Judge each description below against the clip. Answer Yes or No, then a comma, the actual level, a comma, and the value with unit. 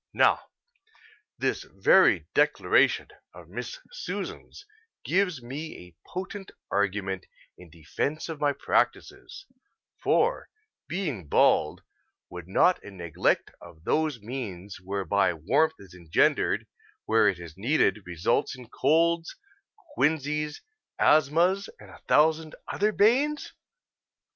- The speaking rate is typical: No, slow, 110 wpm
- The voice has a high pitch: No, medium, 140 Hz